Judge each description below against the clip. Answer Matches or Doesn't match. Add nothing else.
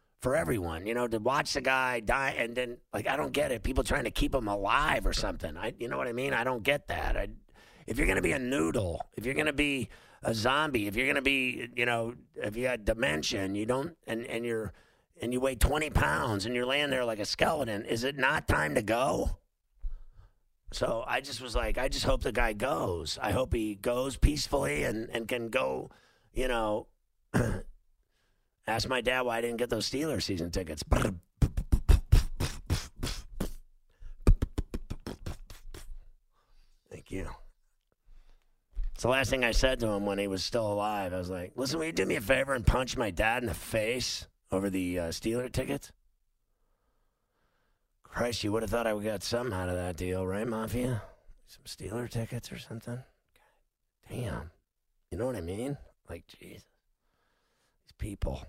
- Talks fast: Doesn't match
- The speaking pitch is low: Matches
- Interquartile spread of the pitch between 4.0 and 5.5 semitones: Matches